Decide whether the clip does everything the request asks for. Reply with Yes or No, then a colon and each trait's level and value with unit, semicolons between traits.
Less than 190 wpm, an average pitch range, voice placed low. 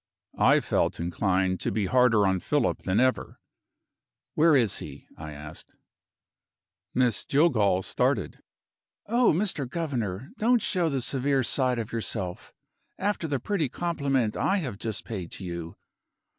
No: average, 140 wpm; wide, 7.8 semitones; low, 125 Hz